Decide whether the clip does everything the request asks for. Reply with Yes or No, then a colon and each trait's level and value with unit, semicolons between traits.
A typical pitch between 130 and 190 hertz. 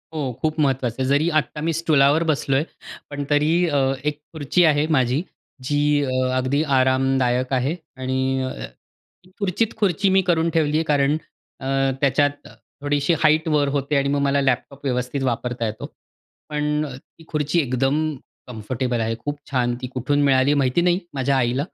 Yes: medium, 140 Hz